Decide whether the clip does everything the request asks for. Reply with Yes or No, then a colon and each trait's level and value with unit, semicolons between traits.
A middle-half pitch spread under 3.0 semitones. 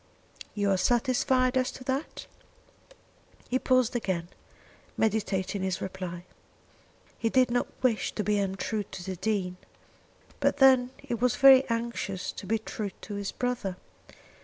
No: average, 4.7 semitones